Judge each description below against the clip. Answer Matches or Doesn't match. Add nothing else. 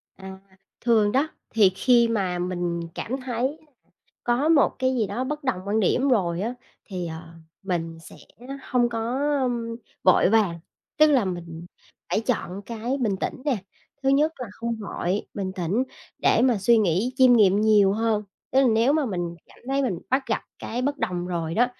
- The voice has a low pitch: Doesn't match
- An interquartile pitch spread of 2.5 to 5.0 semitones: Doesn't match